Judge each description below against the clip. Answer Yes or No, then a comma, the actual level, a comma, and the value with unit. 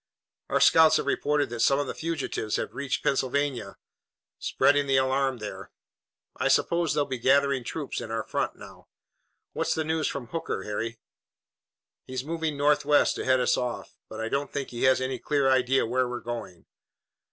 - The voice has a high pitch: No, low, 135 Hz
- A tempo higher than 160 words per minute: Yes, average, 175 wpm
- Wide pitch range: No, average, 2.9 semitones